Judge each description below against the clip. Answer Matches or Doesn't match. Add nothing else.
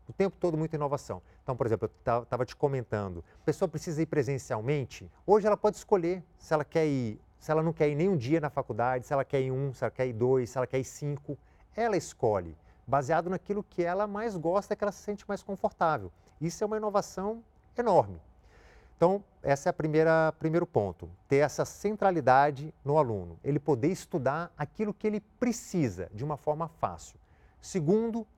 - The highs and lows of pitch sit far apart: Matches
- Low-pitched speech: Doesn't match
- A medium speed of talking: Doesn't match